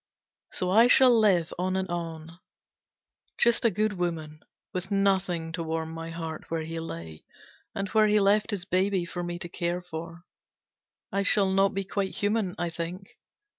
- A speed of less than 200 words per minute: Yes, average, 170 wpm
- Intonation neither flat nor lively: Yes, average, 3.0 semitones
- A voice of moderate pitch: Yes, medium, 180 Hz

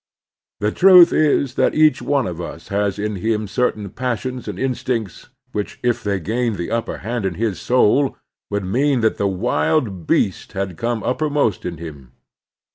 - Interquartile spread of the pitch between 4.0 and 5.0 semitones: Yes, average, 4.6 semitones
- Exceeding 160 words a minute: Yes, average, 170 wpm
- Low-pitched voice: Yes, low, 110 Hz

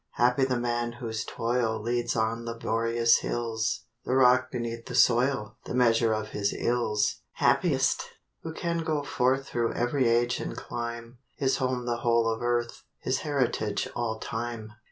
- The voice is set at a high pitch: No, low, 120 Hz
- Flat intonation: Yes, narrow, 1.4 semitones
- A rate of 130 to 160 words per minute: Yes, average, 155 wpm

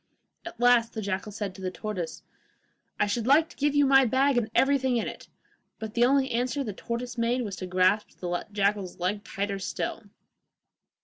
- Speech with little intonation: No, average, 4.4 semitones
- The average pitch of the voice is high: Yes, high, 230 Hz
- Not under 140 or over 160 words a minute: No, average, 190 wpm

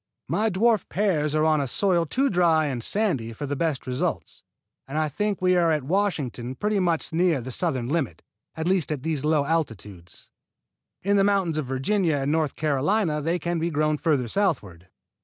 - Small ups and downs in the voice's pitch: No, average, 5.1 semitones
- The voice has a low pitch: No, medium, 155 Hz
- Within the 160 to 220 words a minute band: Yes, average, 180 wpm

